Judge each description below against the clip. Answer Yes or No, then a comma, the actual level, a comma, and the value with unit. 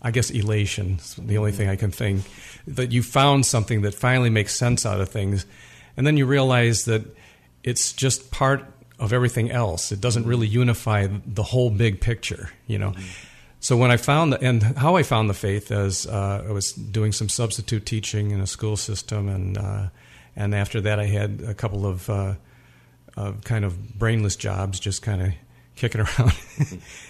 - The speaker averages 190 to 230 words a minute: No, average, 180 wpm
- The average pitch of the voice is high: No, low, 110 Hz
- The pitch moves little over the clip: No, average, 3.5 semitones